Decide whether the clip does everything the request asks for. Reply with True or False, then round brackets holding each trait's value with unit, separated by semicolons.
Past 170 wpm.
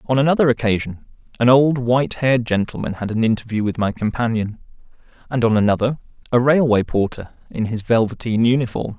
False (160 wpm)